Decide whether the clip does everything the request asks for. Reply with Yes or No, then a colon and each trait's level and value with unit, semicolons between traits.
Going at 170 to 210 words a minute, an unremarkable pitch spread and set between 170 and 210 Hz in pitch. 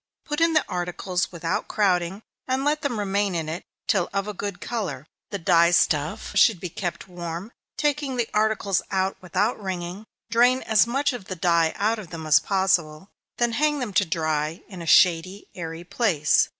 Yes: average, 185 wpm; average, 4.5 semitones; high, 190 Hz